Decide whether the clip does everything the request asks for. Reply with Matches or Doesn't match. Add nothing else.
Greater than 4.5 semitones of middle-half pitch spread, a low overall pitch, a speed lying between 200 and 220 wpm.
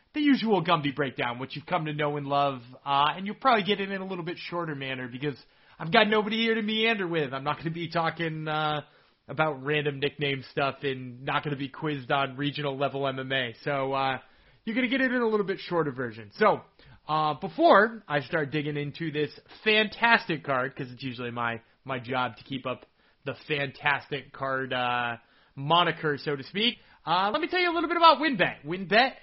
Doesn't match